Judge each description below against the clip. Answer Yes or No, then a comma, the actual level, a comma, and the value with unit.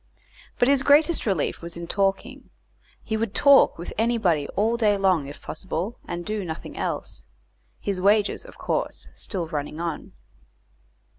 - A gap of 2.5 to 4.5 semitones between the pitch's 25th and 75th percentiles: No, average, 5.0 semitones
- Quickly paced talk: No, average, 150 wpm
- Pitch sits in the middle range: No, high, 195 Hz